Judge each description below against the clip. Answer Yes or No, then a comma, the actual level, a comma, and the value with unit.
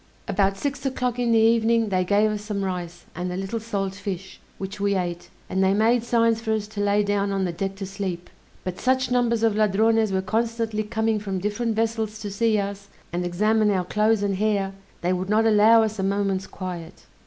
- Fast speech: Yes, fast, 210 wpm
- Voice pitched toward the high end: Yes, high, 205 Hz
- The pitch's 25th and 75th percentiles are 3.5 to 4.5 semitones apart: No, narrow, 2.6 semitones